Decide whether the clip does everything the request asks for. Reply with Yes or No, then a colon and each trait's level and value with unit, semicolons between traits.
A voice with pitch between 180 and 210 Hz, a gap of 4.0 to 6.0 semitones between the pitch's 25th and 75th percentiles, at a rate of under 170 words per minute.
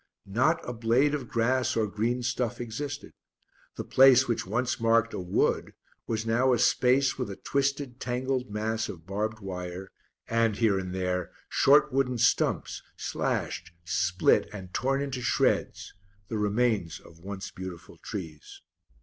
No: low, 115 Hz; average, 4.6 semitones; average, 150 wpm